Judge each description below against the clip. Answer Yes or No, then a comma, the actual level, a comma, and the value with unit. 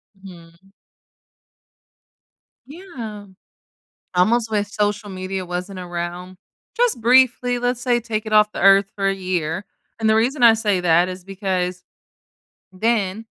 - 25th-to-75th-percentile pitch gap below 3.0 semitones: No, average, 3.7 semitones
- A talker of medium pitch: No, high, 200 Hz